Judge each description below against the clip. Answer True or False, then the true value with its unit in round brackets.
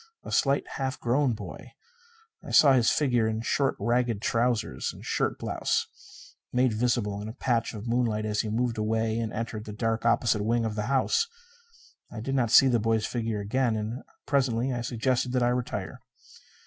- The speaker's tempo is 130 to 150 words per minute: False (185 wpm)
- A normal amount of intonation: False (2.2 semitones)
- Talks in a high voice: False (115 Hz)